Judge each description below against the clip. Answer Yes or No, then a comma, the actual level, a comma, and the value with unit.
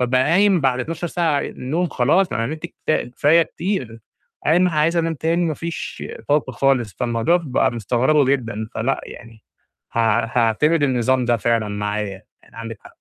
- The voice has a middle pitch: No, low, 130 Hz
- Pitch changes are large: Yes, wide, 5.8 semitones